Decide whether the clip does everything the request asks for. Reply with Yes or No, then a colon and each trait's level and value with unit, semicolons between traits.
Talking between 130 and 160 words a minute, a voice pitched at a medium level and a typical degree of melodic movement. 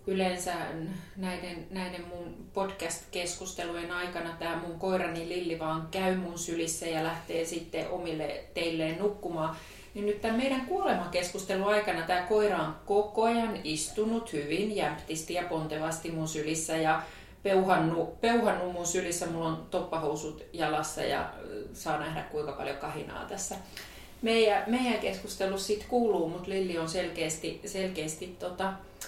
Yes: average, 135 wpm; medium, 180 Hz; average, 3.0 semitones